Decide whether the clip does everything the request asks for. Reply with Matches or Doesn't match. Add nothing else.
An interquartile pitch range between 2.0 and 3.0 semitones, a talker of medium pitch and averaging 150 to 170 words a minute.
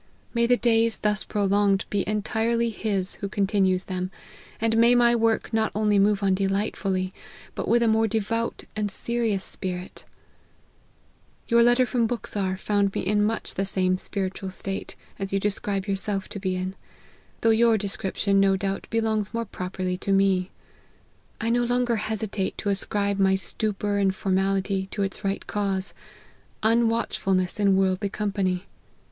Doesn't match